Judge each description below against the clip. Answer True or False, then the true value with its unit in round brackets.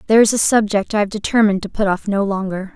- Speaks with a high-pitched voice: True (205 Hz)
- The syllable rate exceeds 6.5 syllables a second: True (7.0 syllables/s)